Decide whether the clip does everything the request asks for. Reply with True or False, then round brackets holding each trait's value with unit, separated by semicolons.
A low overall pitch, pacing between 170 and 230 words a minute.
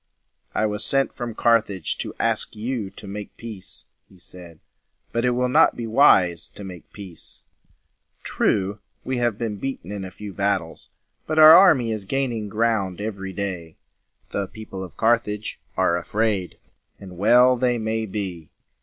False (105 Hz; 160 wpm)